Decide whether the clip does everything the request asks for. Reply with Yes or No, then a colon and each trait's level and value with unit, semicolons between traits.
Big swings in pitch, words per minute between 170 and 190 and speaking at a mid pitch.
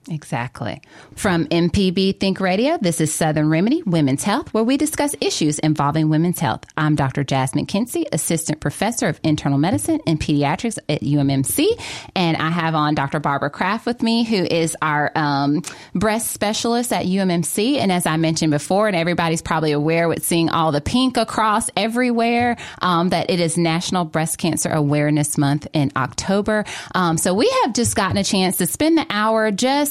Yes: wide, 5.7 semitones; average, 175 wpm; medium, 170 Hz